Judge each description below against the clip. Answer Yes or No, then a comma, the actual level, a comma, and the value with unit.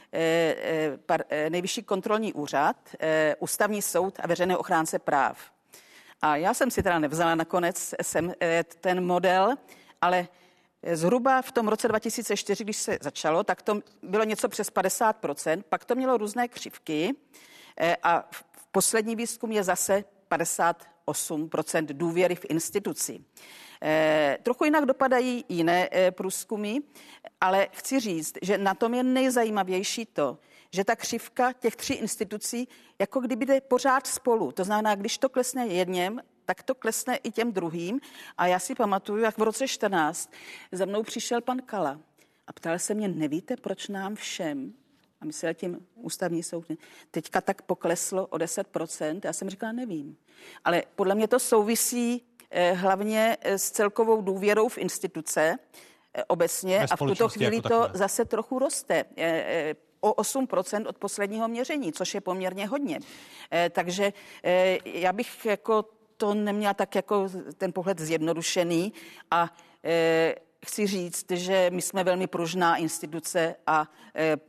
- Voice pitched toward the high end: Yes, high, 195 Hz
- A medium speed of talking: Yes, average, 140 wpm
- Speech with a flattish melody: No, average, 5.0 semitones